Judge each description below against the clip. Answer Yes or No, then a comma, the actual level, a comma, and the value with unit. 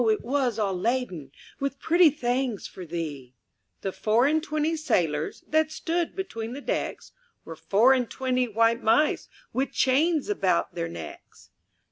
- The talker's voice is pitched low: No, high, 245 Hz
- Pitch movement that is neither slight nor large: No, wide, 7.5 semitones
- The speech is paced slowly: No, average, 150 wpm